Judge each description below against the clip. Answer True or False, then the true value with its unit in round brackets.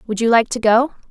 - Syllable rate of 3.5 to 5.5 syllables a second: False (6.1 syllables/s)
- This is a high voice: True (230 Hz)